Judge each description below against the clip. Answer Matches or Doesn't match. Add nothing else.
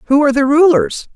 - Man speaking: Doesn't match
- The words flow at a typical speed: Doesn't match